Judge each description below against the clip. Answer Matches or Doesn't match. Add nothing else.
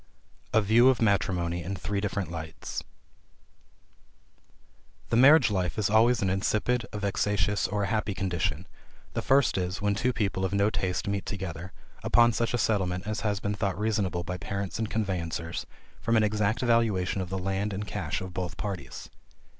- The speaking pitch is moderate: Doesn't match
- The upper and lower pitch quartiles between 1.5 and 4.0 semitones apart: Matches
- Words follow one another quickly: Doesn't match